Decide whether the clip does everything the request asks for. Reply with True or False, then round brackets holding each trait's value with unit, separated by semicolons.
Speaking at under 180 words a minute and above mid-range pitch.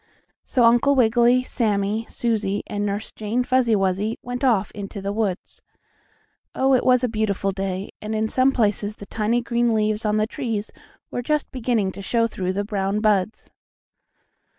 True (170 wpm; 220 Hz)